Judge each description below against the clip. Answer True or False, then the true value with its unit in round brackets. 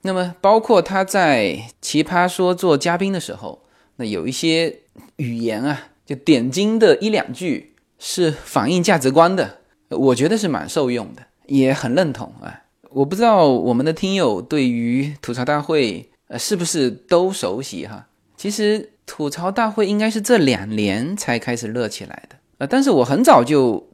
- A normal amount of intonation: False (6.9 semitones)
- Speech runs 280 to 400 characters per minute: False (250 characters per minute)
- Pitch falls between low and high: True (170 Hz)